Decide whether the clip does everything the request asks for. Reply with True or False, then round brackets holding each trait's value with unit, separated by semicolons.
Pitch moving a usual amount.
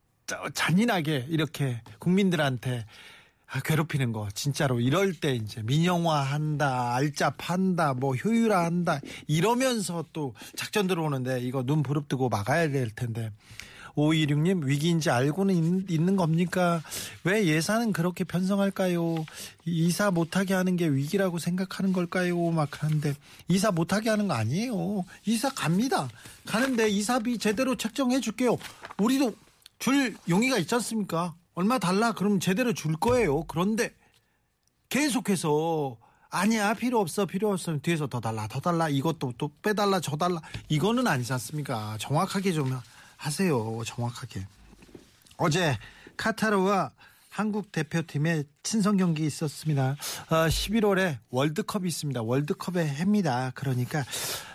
False (5.9 semitones)